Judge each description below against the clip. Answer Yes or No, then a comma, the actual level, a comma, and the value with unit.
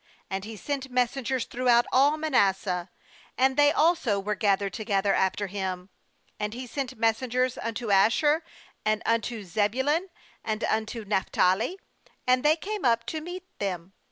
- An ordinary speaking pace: Yes, average, 150 wpm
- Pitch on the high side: Yes, high, 230 Hz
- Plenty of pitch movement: No, average, 4.8 semitones